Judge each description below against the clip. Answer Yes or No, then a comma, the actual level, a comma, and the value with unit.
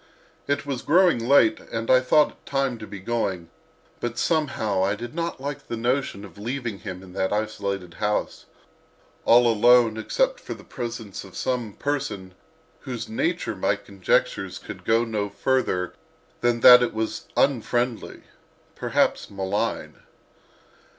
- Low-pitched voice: Yes, low, 120 Hz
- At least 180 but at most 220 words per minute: No, average, 150 wpm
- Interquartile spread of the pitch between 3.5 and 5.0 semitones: Yes, average, 4.5 semitones